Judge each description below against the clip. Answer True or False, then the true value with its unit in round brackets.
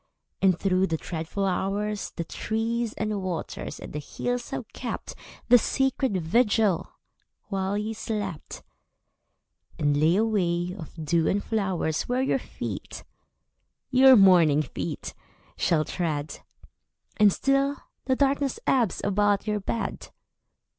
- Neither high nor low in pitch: False (200 Hz)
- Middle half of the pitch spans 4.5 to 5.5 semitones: True (4.8 semitones)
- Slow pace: True (125 wpm)